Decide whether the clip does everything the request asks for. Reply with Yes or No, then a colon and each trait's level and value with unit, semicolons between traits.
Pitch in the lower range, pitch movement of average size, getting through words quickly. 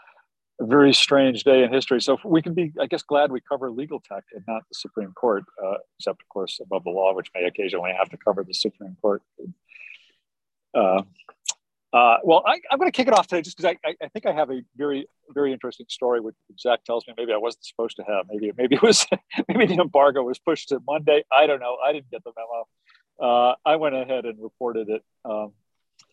Yes: low, 130 Hz; average, 4.5 semitones; fast, 225 wpm